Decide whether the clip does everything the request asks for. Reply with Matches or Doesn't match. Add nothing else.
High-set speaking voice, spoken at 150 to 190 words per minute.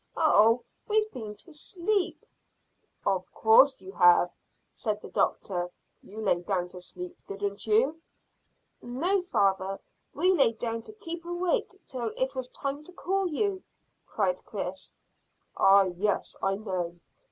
Doesn't match